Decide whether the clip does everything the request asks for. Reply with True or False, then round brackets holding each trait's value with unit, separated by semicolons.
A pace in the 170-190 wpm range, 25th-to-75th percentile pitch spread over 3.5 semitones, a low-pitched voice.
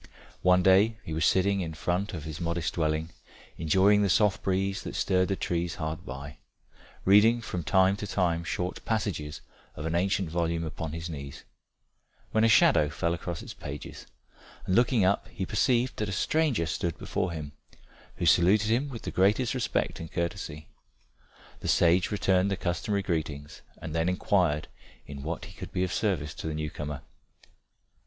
True (175 wpm; 3.9 semitones; 90 Hz)